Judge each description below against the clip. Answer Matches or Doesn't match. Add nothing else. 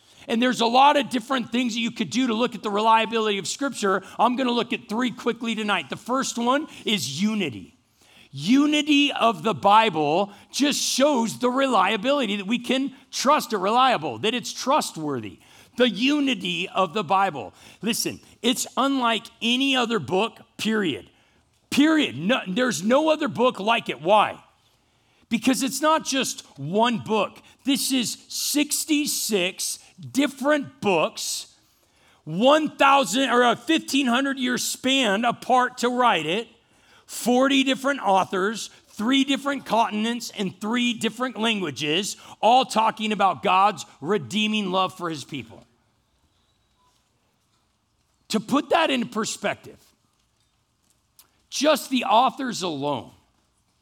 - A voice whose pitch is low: Doesn't match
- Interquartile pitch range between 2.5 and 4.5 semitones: Doesn't match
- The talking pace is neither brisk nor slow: Doesn't match